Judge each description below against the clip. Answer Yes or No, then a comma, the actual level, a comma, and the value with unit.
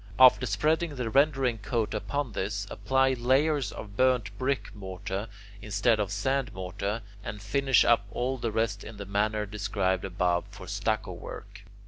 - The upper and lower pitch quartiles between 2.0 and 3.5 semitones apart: No, average, 4.3 semitones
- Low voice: Yes, low, 110 Hz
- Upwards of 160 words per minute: No, average, 155 wpm